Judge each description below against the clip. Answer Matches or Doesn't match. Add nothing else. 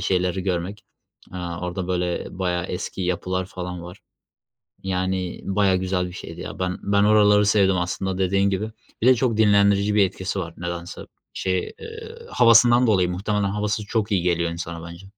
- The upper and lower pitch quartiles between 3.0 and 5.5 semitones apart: Doesn't match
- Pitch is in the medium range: Doesn't match